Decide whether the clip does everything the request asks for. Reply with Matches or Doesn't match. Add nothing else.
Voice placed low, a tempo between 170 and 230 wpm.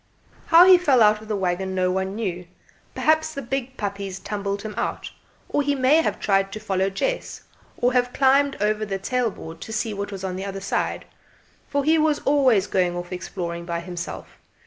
Doesn't match